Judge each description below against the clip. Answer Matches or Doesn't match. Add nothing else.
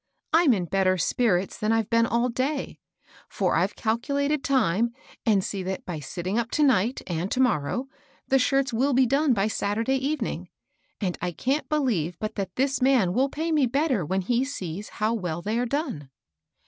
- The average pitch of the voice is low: Doesn't match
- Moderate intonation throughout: Doesn't match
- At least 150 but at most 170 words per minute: Doesn't match